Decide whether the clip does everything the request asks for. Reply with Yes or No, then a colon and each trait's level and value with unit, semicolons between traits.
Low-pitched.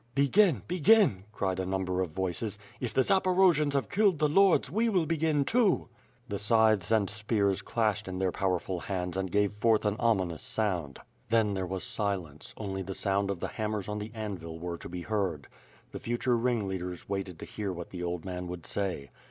Yes: low, 100 Hz